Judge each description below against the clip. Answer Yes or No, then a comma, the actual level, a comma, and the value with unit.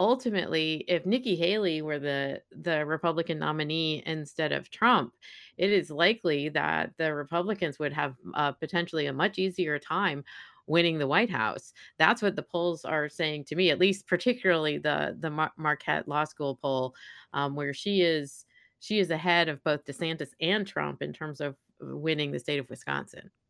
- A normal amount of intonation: Yes, average, 3.1 semitones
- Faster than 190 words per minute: No, average, 175 wpm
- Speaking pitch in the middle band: Yes, medium, 160 Hz